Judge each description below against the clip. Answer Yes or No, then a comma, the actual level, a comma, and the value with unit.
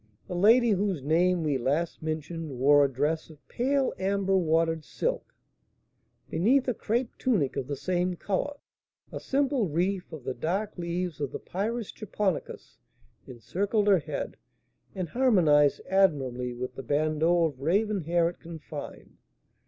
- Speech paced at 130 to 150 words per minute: Yes, average, 145 wpm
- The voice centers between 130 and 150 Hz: No, medium, 175 Hz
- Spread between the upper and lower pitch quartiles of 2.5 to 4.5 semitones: No, average, 5.2 semitones